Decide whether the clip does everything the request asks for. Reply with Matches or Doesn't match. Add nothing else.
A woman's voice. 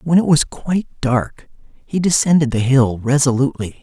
Doesn't match